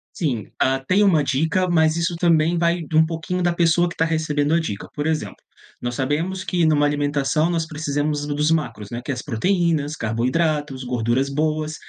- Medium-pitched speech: Yes, medium, 155 Hz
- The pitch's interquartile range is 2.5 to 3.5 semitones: Yes, average, 2.9 semitones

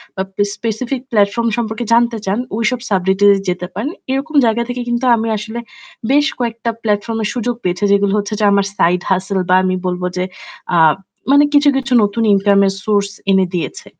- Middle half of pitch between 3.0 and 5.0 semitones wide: Yes, average, 3.5 semitones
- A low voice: No, high, 210 Hz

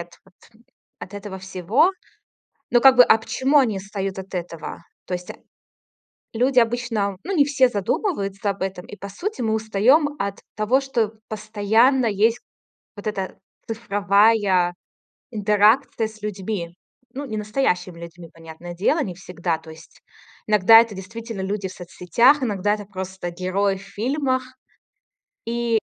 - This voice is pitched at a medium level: No, high, 205 Hz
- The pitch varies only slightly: No, average, 3.6 semitones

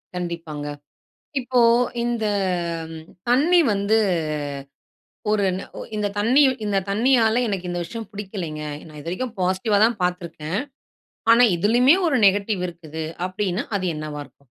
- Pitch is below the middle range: No, high, 195 Hz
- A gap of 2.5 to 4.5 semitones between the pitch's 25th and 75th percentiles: No, average, 5.1 semitones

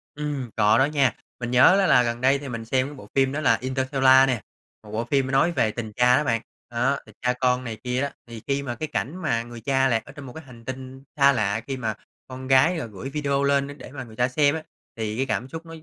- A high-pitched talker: No, low, 130 Hz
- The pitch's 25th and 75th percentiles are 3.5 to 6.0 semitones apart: No, average, 2.9 semitones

